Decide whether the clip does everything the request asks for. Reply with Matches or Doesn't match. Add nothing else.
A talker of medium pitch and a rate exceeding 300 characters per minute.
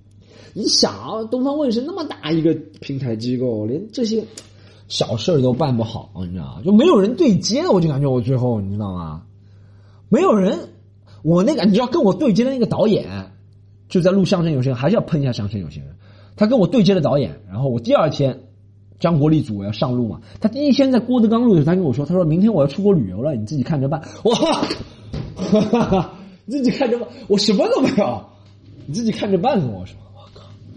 Matches